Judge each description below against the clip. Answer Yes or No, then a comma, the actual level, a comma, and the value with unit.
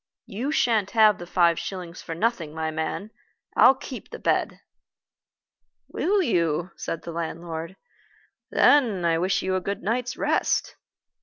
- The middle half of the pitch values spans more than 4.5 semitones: Yes, average, 5.0 semitones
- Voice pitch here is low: No, medium, 185 Hz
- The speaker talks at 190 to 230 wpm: No, average, 145 wpm